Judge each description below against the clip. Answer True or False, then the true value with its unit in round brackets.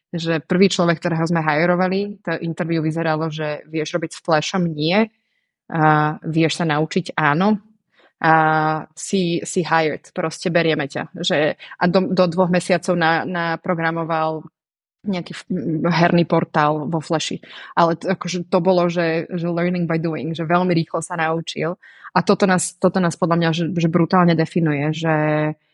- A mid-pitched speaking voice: True (170 Hz)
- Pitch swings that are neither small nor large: False (2.2 semitones)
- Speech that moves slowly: False (160 wpm)